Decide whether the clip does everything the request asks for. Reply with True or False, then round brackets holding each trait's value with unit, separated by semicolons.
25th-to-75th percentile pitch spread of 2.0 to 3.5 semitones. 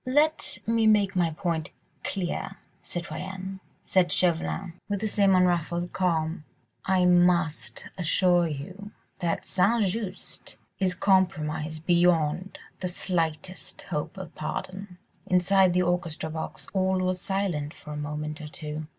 True (2.9 semitones)